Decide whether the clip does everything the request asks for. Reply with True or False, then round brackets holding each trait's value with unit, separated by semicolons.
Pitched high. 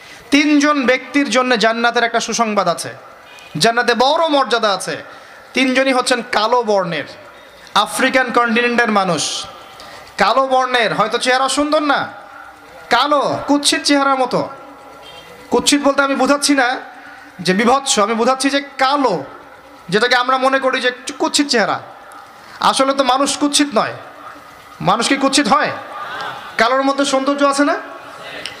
True (260 Hz)